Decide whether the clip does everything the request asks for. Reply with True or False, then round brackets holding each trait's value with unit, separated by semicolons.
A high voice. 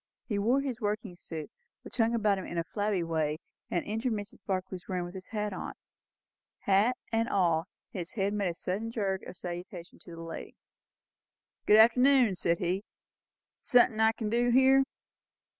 True (205 Hz)